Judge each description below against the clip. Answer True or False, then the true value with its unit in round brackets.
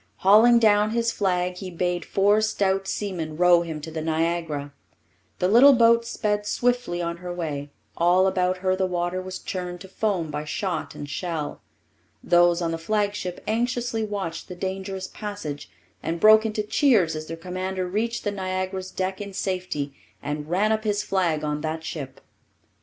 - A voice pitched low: False (185 Hz)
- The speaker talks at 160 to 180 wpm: True (170 wpm)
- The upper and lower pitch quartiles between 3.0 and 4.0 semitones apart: True (3.6 semitones)